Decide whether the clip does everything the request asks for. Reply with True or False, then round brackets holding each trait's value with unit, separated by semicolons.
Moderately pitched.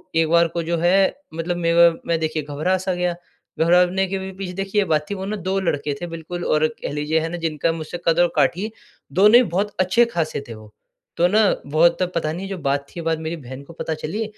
True (170 Hz)